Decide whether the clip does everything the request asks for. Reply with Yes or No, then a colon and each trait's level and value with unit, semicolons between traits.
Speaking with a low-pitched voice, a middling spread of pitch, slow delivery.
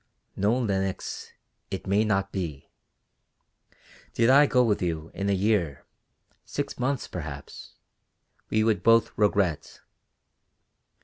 Yes: low, 100 Hz; average, 3.9 semitones; slow, 115 wpm